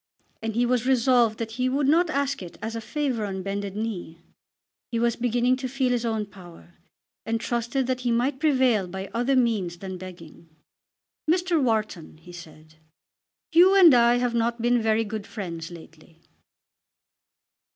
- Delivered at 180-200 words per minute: No, average, 165 wpm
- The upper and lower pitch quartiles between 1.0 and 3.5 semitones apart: No, average, 4.8 semitones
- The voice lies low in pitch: No, high, 230 Hz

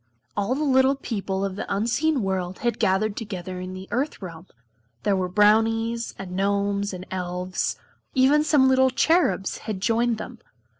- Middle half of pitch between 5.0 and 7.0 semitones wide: No, average, 4.6 semitones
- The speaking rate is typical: Yes, average, 160 wpm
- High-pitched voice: Yes, high, 205 Hz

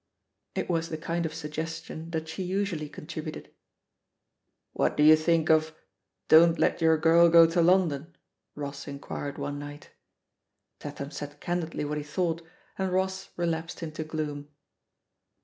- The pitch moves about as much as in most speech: No, narrow, 2.1 semitones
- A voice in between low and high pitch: Yes, medium, 160 Hz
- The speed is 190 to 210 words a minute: No, average, 150 wpm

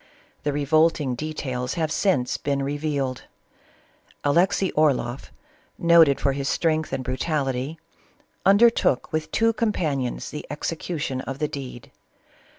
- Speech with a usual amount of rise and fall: Yes, average, 3.3 semitones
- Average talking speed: No, slow, 120 wpm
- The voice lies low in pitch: No, medium, 145 Hz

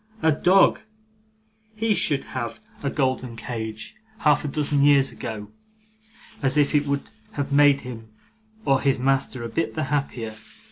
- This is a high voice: No, medium, 140 Hz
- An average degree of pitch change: Yes, average, 3.3 semitones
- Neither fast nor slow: Yes, average, 150 wpm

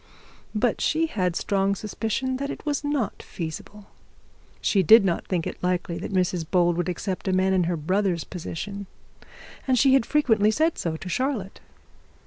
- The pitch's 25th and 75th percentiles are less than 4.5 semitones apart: No, average, 5.2 semitones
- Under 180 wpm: Yes, average, 170 wpm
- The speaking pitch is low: No, high, 195 Hz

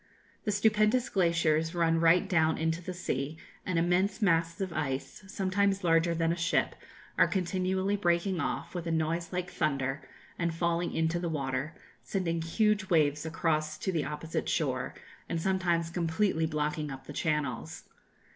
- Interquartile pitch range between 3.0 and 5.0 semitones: No, narrow, 2.6 semitones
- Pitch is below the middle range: No, medium, 170 Hz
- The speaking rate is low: No, average, 155 wpm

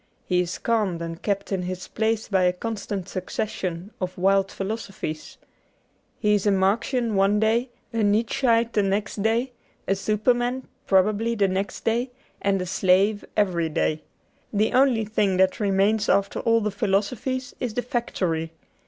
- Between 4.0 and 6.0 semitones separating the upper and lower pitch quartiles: No, average, 3.1 semitones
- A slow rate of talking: No, average, 160 wpm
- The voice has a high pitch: Yes, high, 205 Hz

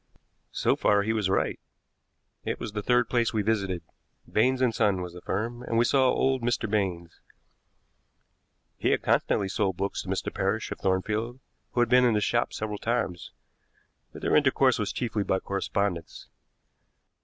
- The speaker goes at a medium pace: Yes, average, 170 wpm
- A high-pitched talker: No, low, 110 Hz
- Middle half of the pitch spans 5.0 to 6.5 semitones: No, average, 3.5 semitones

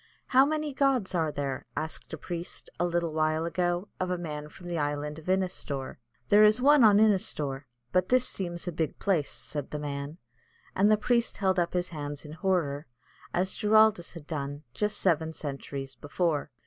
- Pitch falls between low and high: Yes, medium, 170 Hz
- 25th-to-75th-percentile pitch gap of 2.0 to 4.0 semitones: No, average, 4.6 semitones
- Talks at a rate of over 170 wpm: Yes, average, 180 wpm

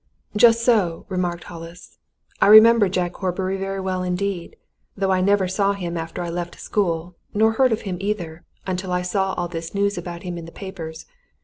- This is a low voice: No, medium, 185 Hz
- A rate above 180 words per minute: Yes, average, 190 wpm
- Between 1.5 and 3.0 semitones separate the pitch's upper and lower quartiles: Yes, narrow, 2.4 semitones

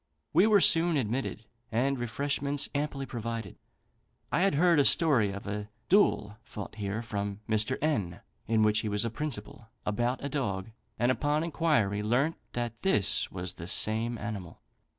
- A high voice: No, low, 115 Hz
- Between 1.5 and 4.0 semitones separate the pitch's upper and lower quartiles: No, wide, 5.4 semitones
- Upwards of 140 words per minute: Yes, average, 160 wpm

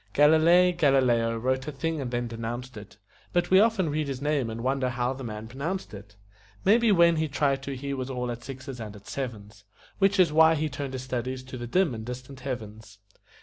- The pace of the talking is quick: Yes, fast, 215 wpm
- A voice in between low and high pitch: No, low, 130 Hz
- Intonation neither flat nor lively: Yes, average, 4.2 semitones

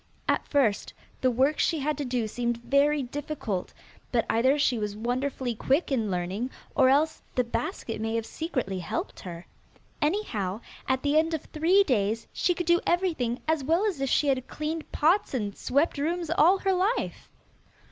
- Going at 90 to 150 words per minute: No, average, 180 wpm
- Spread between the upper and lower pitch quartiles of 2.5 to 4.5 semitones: No, wide, 5.5 semitones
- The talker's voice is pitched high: Yes, very high, 270 Hz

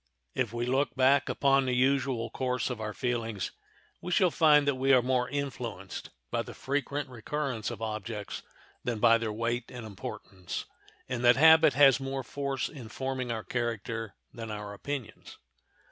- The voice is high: No, low, 125 Hz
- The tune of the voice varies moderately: Yes, average, 3.2 semitones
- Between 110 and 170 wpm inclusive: Yes, average, 165 wpm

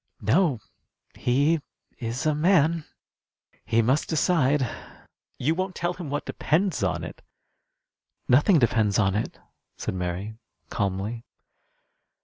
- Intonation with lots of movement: Yes, wide, 6.7 semitones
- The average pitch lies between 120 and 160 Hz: Yes, low, 135 Hz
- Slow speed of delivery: Yes, slow, 115 wpm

